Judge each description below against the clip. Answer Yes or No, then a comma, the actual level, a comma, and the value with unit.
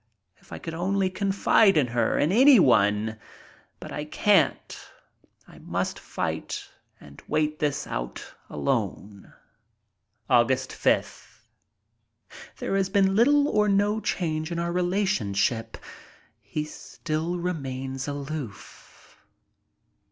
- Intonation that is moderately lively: No, wide, 7.2 semitones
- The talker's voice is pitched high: No, medium, 155 Hz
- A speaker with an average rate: No, slow, 105 wpm